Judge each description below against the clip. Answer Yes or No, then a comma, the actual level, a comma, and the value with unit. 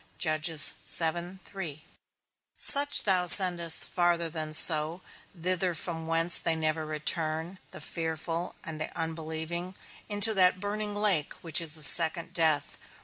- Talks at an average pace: No, slow, 120 wpm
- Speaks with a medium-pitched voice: Yes, medium, 165 Hz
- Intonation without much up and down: Yes, narrow, 2.3 semitones